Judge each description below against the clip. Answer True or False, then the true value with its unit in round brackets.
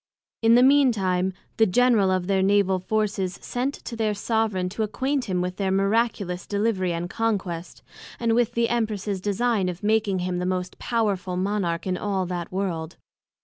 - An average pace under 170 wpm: False (180 wpm)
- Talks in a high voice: True (200 Hz)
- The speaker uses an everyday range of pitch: True (3.5 semitones)